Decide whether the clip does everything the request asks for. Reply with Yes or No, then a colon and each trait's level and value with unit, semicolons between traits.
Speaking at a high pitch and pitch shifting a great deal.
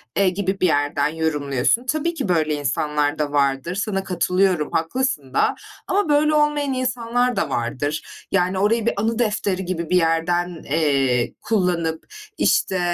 No: medium, 180 Hz; wide, 7.2 semitones